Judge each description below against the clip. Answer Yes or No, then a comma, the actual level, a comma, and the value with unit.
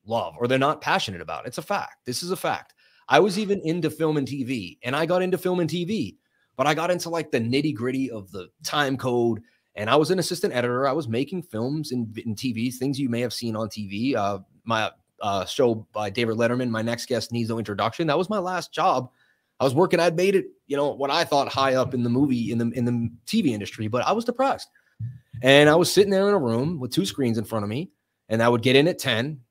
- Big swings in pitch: Yes, wide, 6.0 semitones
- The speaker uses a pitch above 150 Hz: No, low, 135 Hz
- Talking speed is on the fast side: Yes, fast, 255 wpm